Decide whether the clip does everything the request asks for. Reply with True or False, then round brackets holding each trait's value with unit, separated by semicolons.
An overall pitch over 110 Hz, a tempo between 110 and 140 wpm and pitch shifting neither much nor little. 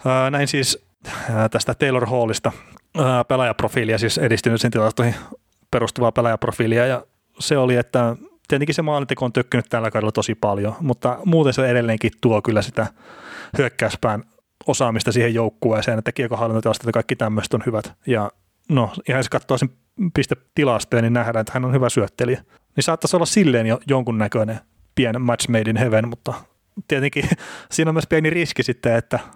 False (125 Hz; 155 wpm; 3.0 semitones)